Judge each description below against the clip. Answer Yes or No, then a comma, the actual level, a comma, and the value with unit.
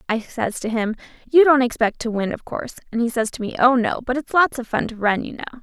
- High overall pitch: Yes, high, 240 Hz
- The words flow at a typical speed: No, fast, 290 wpm